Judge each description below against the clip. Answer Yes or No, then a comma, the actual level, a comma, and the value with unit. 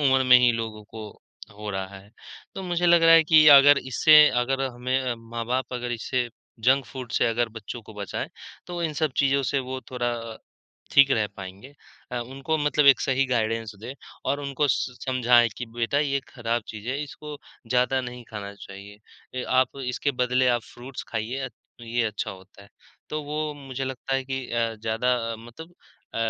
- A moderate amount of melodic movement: Yes, average, 3.1 semitones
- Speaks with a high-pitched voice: No, low, 125 Hz